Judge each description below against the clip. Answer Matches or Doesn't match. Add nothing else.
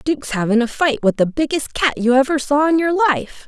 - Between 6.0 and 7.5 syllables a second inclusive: Doesn't match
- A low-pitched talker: Doesn't match